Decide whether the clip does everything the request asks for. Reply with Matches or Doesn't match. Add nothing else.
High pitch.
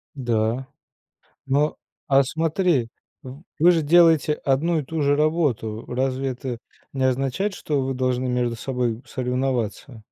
Doesn't match